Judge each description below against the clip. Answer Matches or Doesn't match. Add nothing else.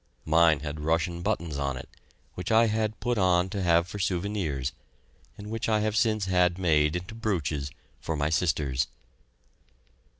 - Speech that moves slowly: Doesn't match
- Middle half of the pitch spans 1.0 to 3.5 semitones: Doesn't match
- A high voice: Doesn't match